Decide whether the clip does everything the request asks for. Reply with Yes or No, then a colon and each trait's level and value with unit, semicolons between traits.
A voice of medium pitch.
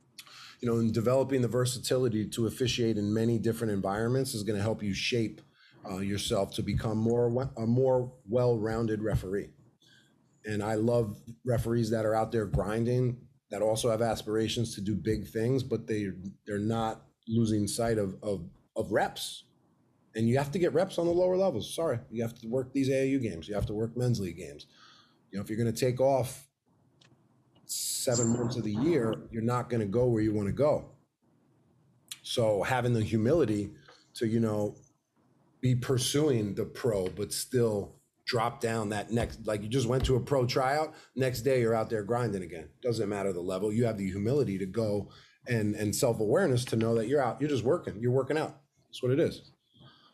No: low, 115 Hz